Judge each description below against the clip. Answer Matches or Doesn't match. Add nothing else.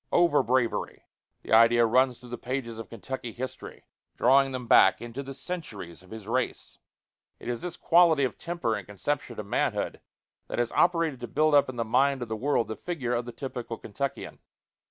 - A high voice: Doesn't match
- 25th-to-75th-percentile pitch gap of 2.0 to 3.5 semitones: Matches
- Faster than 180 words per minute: Matches